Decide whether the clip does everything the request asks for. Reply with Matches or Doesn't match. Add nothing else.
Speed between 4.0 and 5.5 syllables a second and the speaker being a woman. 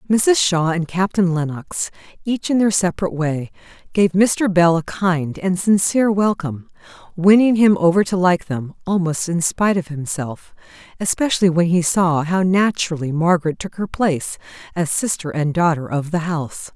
Matches